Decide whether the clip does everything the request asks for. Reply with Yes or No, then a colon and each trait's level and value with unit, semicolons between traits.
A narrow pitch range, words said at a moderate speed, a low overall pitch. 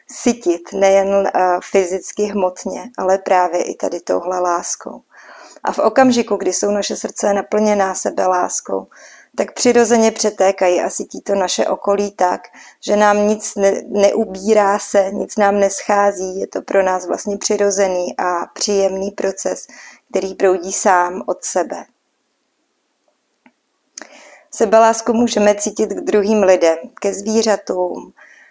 No: narrow, 2.0 semitones; average, 125 wpm; high, 200 Hz